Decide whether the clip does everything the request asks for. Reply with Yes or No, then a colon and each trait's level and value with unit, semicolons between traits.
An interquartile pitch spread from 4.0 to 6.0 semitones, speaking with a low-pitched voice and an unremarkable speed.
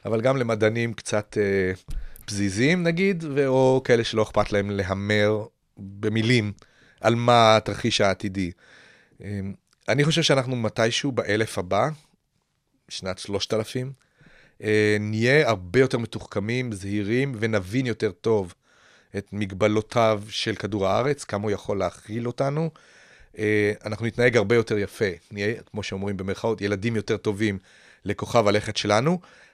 No: average, 3.1 semitones; low, 110 Hz; average, 130 wpm